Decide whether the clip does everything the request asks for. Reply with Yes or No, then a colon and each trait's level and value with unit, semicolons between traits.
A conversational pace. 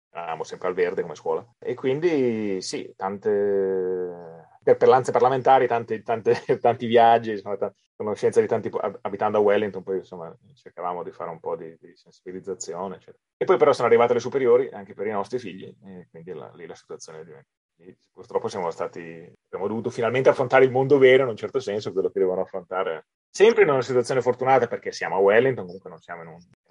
No: fast, 195 wpm